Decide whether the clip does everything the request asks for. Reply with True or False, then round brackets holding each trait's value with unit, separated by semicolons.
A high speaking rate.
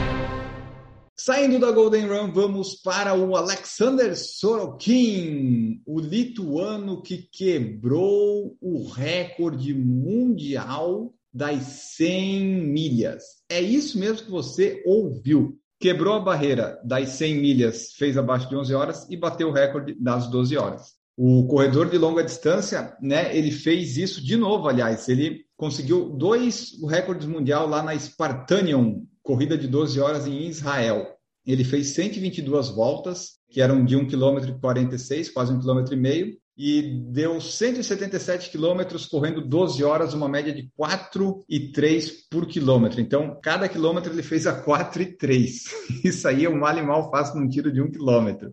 False (150 wpm)